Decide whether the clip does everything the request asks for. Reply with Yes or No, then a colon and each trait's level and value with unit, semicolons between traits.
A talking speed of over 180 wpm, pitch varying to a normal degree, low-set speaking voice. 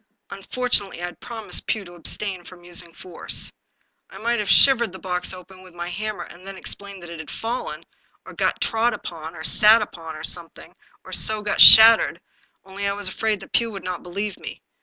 No: average, 200 wpm; average, 3.5 semitones; high, 195 Hz